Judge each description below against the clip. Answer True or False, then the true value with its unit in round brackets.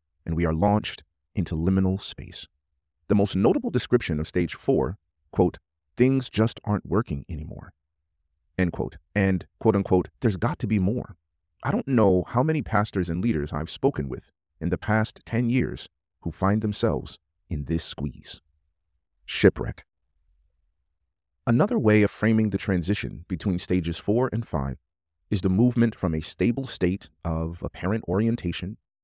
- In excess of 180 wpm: False (155 wpm)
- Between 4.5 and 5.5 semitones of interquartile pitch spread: True (5.1 semitones)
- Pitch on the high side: False (90 Hz)